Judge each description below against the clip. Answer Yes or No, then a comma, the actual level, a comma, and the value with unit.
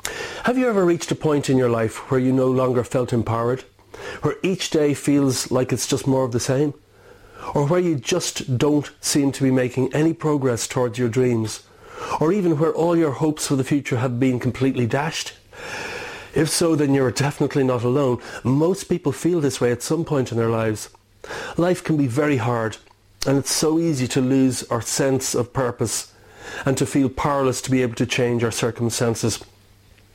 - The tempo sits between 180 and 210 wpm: Yes, average, 195 wpm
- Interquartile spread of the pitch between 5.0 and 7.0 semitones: No, average, 3.7 semitones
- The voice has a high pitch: No, low, 135 Hz